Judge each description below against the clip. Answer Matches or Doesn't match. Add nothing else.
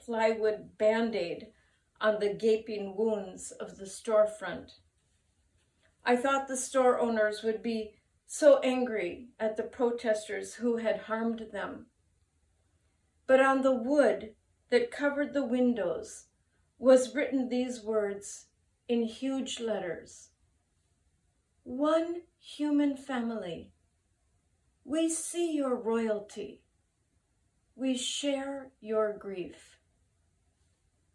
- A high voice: Matches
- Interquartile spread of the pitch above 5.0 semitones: Matches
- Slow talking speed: Matches